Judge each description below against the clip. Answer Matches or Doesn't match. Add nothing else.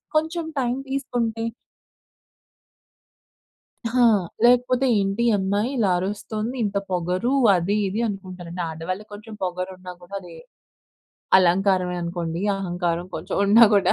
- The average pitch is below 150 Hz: Doesn't match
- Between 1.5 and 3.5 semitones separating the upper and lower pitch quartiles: Doesn't match